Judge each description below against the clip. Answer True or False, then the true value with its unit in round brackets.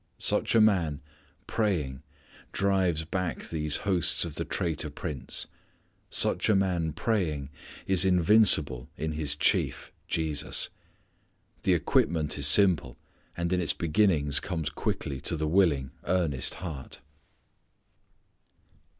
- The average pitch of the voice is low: True (80 Hz)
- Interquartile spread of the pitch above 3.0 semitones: True (4.0 semitones)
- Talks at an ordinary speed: False (115 wpm)